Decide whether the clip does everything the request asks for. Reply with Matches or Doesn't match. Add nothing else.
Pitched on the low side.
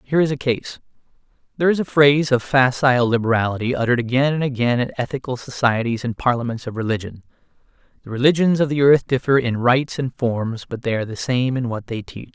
Matches